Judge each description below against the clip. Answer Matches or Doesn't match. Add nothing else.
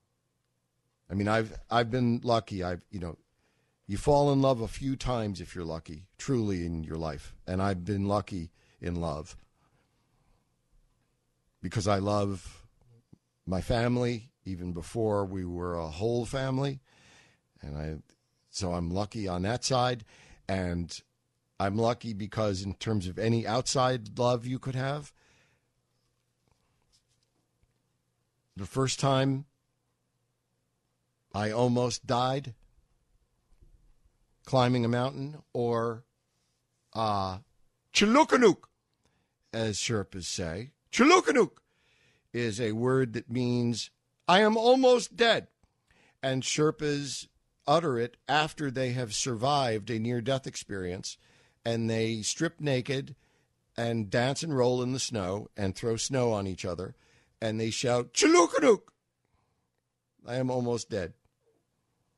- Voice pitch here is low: Matches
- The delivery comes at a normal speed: Doesn't match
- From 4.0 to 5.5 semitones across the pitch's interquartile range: Matches